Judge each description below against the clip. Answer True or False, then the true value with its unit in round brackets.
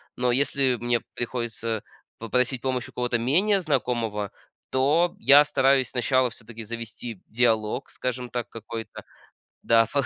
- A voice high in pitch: False (120 Hz)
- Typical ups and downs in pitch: False (2.3 semitones)